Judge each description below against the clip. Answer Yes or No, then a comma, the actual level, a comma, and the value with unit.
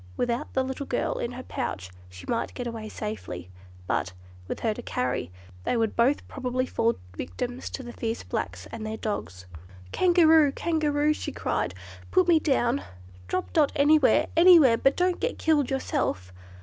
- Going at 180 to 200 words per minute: No, average, 165 wpm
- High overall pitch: Yes, very high, 250 Hz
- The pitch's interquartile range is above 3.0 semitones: Yes, average, 5.2 semitones